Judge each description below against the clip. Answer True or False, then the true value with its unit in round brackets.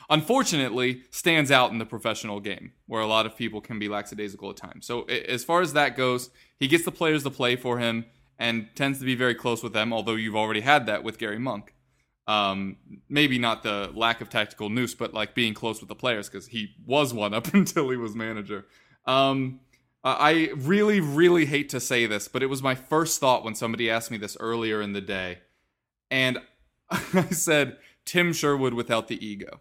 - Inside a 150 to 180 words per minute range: False (205 wpm)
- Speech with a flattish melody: False (4.2 semitones)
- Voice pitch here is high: False (125 Hz)